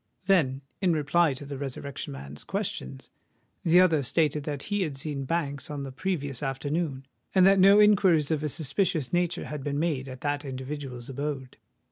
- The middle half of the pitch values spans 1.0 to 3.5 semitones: No, average, 3.9 semitones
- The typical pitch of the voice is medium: Yes, medium, 145 Hz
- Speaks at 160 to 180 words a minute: Yes, average, 175 wpm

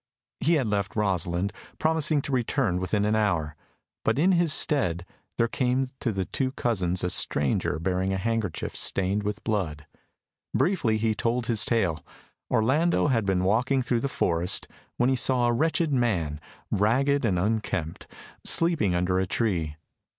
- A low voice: Yes, low, 110 Hz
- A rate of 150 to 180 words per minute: Yes, average, 160 wpm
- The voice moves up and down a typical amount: No, wide, 5.9 semitones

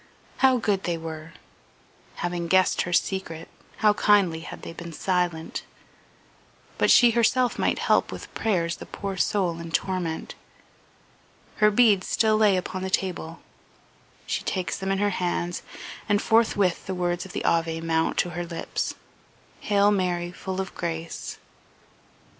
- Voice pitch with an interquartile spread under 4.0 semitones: Yes, average, 3.3 semitones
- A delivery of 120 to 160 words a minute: Yes, average, 145 wpm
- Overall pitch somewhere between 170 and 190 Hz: Yes, medium, 185 Hz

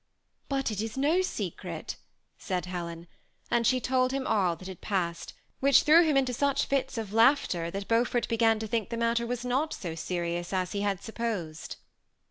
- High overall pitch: Yes, high, 225 Hz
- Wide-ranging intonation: Yes, wide, 5.8 semitones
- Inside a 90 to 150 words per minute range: No, average, 190 wpm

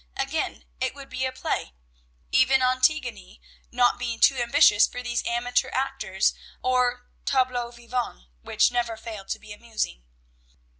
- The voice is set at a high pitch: Yes, high, 245 Hz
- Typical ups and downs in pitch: No, narrow, 2.1 semitones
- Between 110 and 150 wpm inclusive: Yes, average, 140 wpm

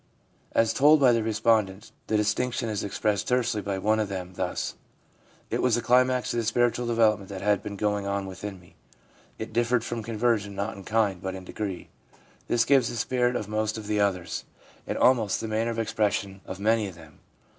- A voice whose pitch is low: Yes, low, 110 Hz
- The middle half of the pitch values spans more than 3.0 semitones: No, average, 2.7 semitones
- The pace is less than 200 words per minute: No, fast, 205 wpm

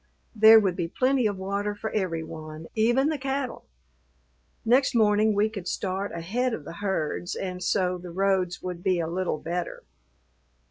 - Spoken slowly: No, average, 170 wpm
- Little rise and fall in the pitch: No, average, 3.7 semitones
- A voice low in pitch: No, high, 195 Hz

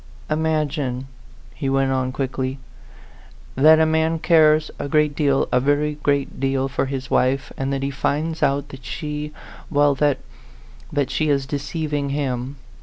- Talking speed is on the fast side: No, average, 155 wpm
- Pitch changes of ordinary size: No, narrow, 2.1 semitones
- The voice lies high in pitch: No, medium, 145 Hz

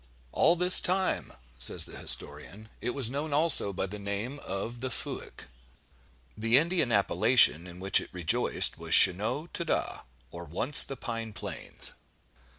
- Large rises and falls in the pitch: Yes, wide, 6.6 semitones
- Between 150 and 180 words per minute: Yes, average, 155 wpm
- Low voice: Yes, low, 115 Hz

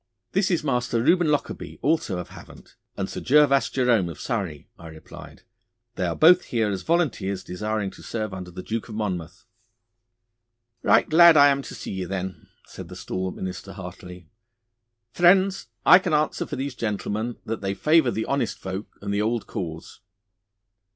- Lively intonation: Yes, wide, 7.3 semitones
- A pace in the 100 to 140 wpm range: No, average, 170 wpm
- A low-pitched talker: Yes, low, 110 Hz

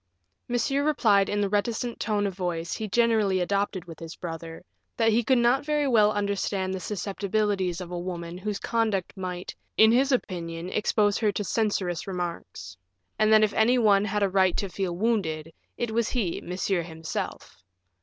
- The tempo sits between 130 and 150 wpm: No, average, 175 wpm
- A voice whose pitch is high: Yes, high, 200 Hz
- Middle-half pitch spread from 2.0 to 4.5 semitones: Yes, average, 3.6 semitones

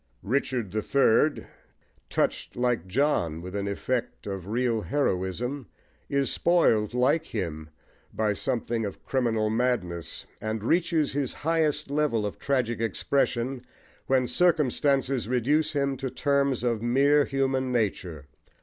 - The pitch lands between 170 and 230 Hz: No, low, 125 Hz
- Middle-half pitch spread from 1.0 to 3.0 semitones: No, average, 4.4 semitones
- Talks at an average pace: No, slow, 125 wpm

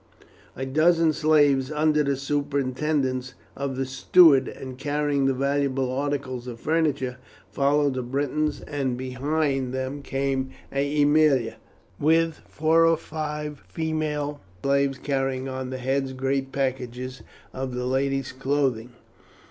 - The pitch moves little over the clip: Yes, narrow, 2.2 semitones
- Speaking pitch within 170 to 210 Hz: No, medium, 140 Hz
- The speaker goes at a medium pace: No, slow, 120 wpm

